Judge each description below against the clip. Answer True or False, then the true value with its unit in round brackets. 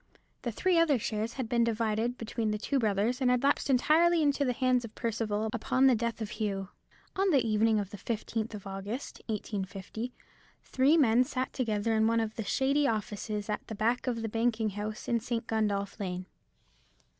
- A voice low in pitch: False (225 Hz)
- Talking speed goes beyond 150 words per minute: True (190 wpm)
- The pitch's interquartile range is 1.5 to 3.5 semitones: True (3.0 semitones)